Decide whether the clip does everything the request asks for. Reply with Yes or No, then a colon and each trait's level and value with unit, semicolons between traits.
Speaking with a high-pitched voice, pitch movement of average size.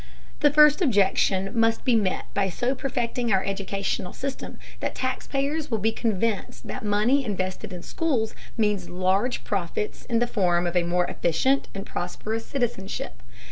Yes: high, 215 Hz; average, 4.7 semitones